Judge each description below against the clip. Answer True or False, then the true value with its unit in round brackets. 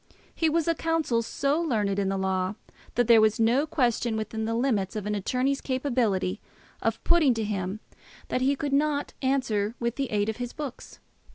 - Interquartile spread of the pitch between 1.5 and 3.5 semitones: False (4.8 semitones)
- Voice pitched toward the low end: False (235 Hz)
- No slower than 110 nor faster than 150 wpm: False (190 wpm)